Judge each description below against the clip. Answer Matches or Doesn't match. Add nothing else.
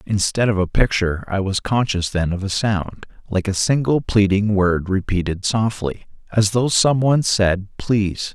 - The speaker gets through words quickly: Doesn't match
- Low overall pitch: Matches